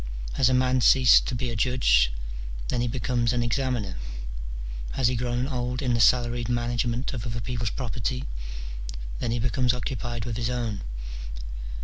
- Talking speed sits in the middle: Yes, average, 160 wpm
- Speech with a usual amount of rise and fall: No, narrow, 1.3 semitones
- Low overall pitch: Yes, low, 120 Hz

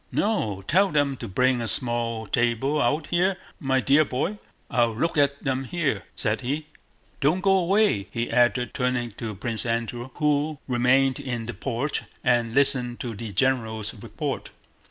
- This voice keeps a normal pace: Yes, average, 160 wpm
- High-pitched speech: No, low, 125 Hz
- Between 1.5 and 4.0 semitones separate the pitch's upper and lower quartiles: Yes, average, 3.7 semitones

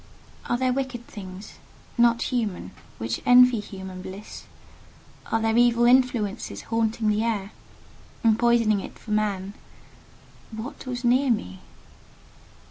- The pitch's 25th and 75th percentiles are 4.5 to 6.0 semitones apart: No, average, 2.8 semitones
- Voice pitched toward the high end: Yes, high, 225 Hz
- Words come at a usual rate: No, slow, 125 wpm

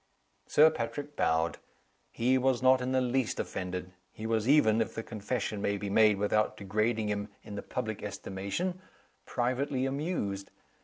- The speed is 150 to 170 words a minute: Yes, average, 155 wpm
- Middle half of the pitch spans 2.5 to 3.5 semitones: No, average, 4.3 semitones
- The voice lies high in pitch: No, low, 115 Hz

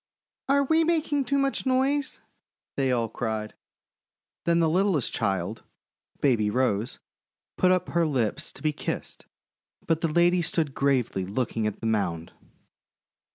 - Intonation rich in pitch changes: Yes, wide, 8.8 semitones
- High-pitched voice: No, medium, 145 Hz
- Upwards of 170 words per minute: No, average, 140 wpm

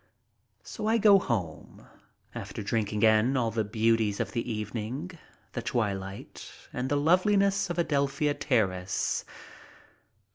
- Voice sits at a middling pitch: No, low, 115 Hz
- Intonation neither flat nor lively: No, wide, 5.9 semitones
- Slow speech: Yes, slow, 130 wpm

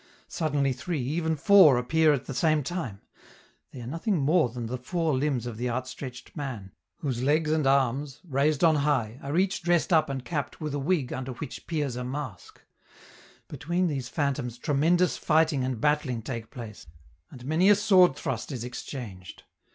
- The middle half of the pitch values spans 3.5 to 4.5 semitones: Yes, average, 4.1 semitones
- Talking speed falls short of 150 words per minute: No, average, 175 wpm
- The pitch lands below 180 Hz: Yes, medium, 140 Hz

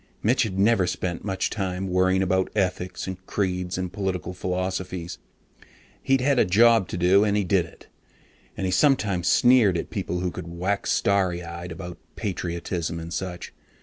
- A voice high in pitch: No, very low, 95 Hz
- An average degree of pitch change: No, narrow, 2.0 semitones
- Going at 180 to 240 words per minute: No, average, 170 wpm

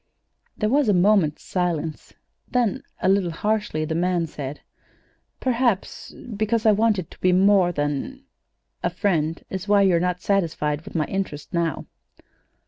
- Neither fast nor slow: Yes, average, 145 wpm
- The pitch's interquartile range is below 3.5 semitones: No, average, 4.2 semitones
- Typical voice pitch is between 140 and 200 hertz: Yes, medium, 185 Hz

